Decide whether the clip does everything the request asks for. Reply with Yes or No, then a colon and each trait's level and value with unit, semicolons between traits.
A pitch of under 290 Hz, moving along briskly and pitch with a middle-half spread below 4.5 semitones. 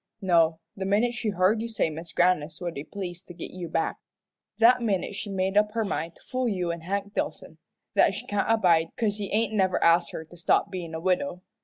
Yes: medium, 185 Hz; fast, 225 wpm; average, 3.7 semitones